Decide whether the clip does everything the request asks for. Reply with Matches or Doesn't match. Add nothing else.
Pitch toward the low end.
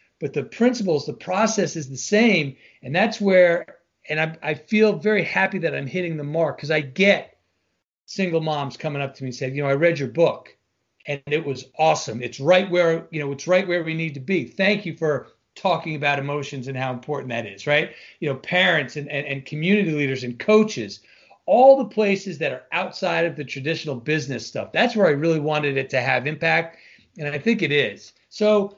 Doesn't match